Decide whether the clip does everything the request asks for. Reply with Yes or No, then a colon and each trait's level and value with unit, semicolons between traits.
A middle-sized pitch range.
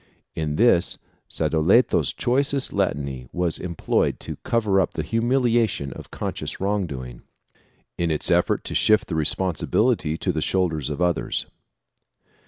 No: wide, 6.7 semitones